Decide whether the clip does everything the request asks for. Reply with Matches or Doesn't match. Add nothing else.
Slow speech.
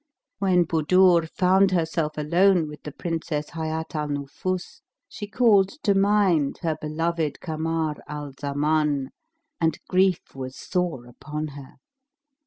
Matches